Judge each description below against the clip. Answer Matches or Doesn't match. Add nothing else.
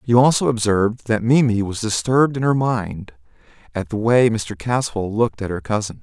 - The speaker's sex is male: Matches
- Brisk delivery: Doesn't match